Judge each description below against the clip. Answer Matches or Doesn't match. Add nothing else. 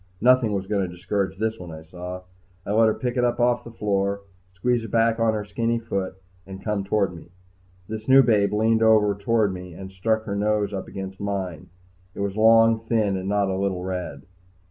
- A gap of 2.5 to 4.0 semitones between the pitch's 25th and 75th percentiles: Matches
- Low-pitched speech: Matches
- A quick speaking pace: Matches